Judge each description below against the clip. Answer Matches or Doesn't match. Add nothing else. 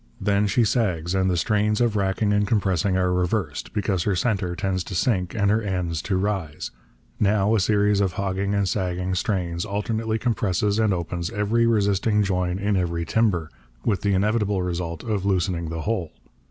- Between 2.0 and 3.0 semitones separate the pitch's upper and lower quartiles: Matches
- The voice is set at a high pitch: Doesn't match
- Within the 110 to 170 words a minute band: Doesn't match